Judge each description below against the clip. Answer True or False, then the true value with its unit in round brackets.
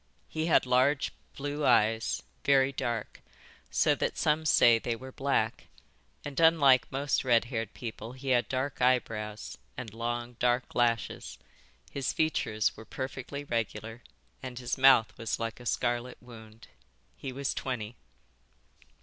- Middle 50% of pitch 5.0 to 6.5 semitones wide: False (2.8 semitones)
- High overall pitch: False (125 Hz)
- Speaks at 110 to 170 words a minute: True (140 wpm)